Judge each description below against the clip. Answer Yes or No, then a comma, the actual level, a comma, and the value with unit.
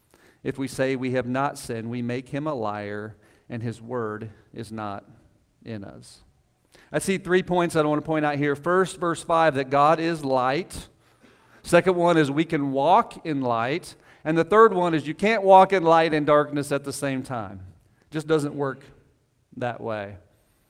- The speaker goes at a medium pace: Yes, average, 190 wpm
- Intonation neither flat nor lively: No, wide, 5.7 semitones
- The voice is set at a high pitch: No, medium, 140 Hz